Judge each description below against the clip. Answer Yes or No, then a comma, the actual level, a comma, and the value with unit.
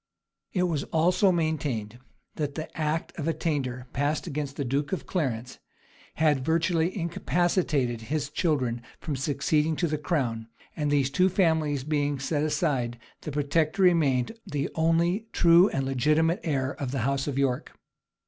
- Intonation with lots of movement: No, average, 3.2 semitones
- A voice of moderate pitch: Yes, medium, 150 Hz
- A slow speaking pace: No, average, 150 wpm